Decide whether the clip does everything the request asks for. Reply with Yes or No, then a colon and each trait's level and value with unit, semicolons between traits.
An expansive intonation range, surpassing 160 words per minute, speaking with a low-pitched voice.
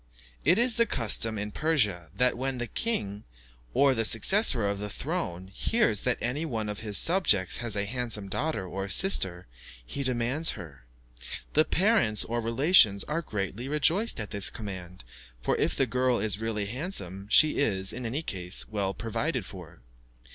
Yes: wide, 6.2 semitones; average, 170 wpm; low, 115 Hz